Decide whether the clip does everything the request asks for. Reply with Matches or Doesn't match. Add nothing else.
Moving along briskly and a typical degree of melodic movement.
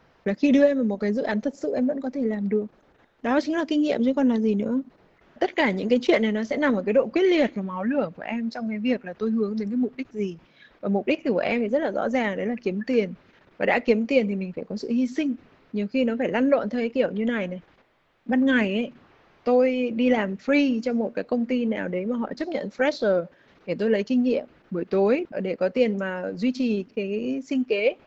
Matches